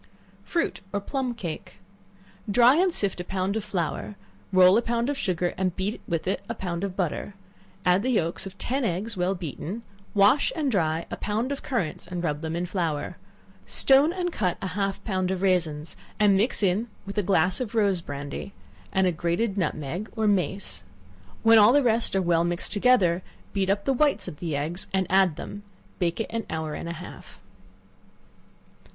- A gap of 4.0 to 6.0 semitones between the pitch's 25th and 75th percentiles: Yes, average, 4.3 semitones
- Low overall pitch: No, high, 190 Hz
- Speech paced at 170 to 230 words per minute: Yes, average, 190 wpm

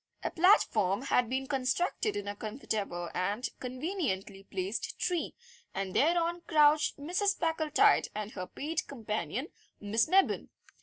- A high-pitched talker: Yes, very high, 260 Hz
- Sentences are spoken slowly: Yes, slow, 130 wpm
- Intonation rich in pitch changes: Yes, wide, 7.9 semitones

